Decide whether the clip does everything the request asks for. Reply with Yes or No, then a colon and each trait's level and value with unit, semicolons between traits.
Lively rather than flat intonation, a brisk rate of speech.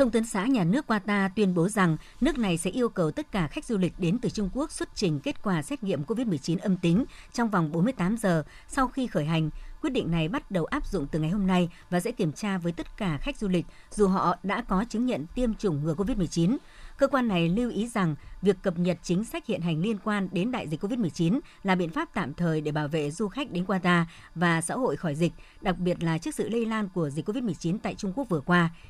No: average, 4.9 semitones; fast, 255 wpm